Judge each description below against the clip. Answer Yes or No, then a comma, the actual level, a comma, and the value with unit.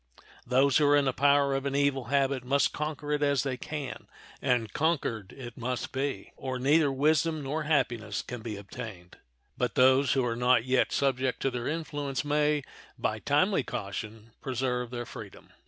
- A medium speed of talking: Yes, average, 175 wpm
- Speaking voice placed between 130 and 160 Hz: Yes, low, 135 Hz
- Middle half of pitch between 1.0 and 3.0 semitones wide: Yes, average, 2.7 semitones